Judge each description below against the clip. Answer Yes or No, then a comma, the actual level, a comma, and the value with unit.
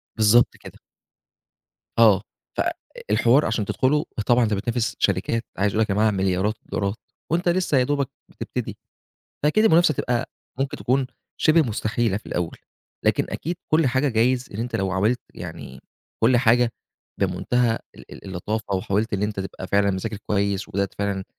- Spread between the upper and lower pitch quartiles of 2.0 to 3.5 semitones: No, average, 4.1 semitones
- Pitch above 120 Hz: No, low, 110 Hz